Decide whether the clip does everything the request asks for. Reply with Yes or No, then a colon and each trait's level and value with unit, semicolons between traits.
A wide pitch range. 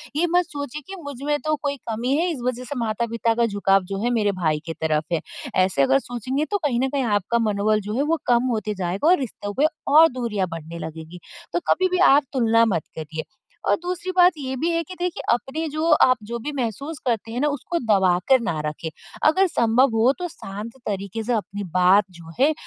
Yes: wide, 6.6 semitones